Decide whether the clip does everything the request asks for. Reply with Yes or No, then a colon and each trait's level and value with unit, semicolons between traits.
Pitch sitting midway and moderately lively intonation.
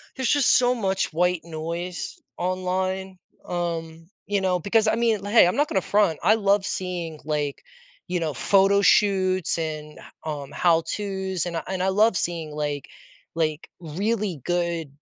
Yes: medium, 180 Hz; average, 3.5 semitones